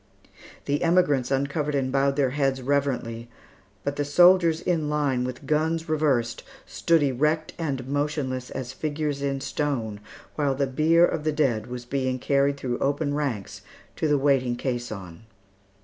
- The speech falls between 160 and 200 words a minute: No, average, 150 wpm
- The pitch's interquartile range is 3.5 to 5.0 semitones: No, average, 2.7 semitones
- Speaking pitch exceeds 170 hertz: No, medium, 140 Hz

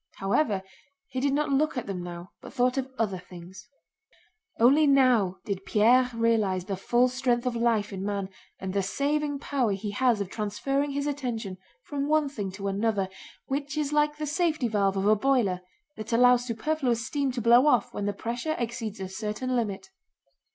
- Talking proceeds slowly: No, average, 185 wpm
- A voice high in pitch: Yes, high, 235 Hz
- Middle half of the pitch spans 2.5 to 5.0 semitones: No, wide, 5.4 semitones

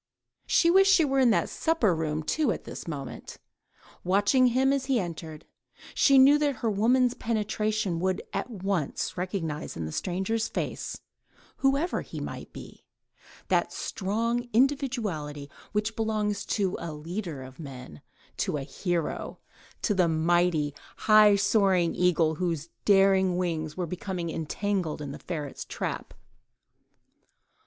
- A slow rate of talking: Yes, slow, 130 wpm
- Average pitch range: No, wide, 5.7 semitones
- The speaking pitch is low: No, high, 190 Hz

